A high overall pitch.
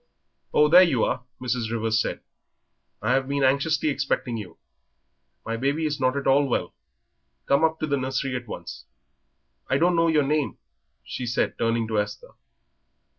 No: low, 135 Hz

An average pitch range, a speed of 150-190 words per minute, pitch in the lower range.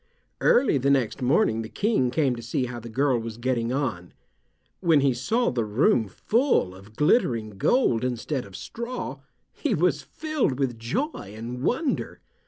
No: wide, 5.9 semitones; average, 165 wpm; low, 125 Hz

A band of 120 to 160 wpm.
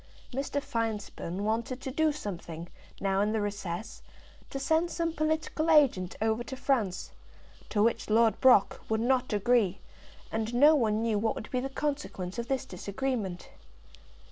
Yes: average, 155 wpm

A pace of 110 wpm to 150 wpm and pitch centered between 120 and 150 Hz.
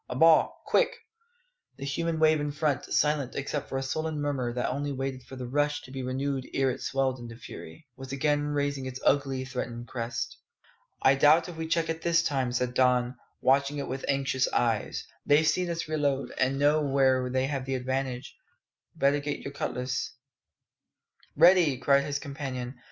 No: average, 185 wpm; low, 135 Hz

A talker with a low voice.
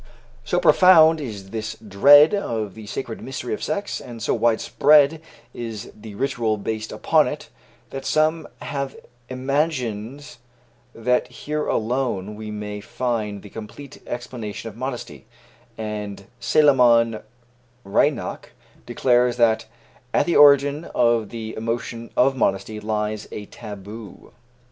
Yes: low, 115 Hz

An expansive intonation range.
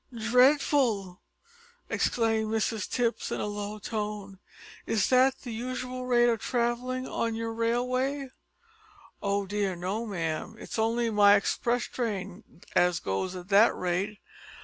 No: average, 3.4 semitones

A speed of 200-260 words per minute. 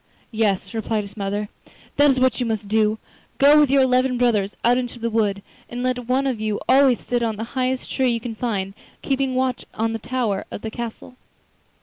Yes: fast, 205 wpm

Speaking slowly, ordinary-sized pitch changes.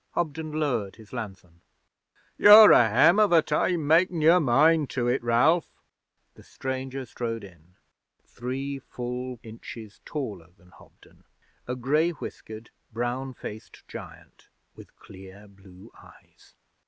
No: slow, 130 wpm; wide, 5.8 semitones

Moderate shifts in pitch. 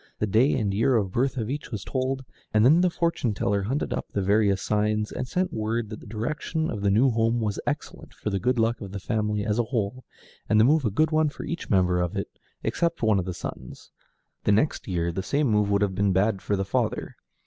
Yes: average, 4.3 semitones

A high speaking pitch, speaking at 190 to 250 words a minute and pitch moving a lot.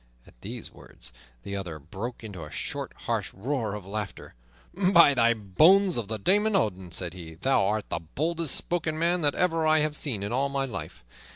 No: low, 120 Hz; average, 195 wpm; wide, 8.4 semitones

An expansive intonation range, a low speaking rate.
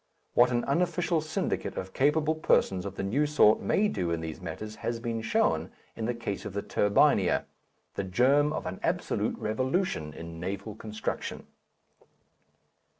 No: wide, 7.0 semitones; average, 155 wpm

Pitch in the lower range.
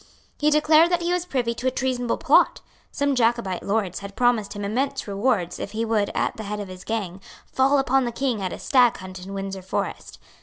No: high, 230 Hz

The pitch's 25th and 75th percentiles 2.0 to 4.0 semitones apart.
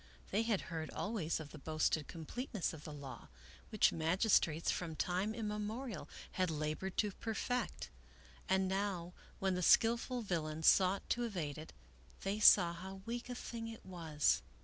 No: average, 5.1 semitones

